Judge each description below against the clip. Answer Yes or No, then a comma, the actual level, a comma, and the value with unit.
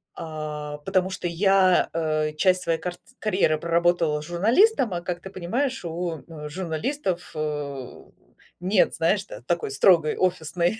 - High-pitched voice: No, medium, 170 Hz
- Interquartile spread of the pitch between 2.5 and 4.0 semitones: Yes, average, 3.3 semitones